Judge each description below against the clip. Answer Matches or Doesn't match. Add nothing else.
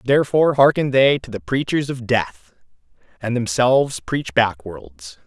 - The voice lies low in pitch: Matches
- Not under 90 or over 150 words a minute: Matches